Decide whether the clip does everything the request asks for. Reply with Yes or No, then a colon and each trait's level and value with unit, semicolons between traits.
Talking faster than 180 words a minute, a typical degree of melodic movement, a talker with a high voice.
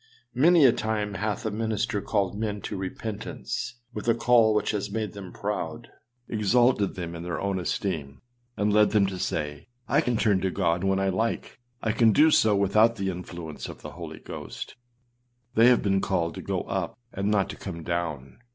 No: average, 195 wpm; average, 3.1 semitones; low, 100 Hz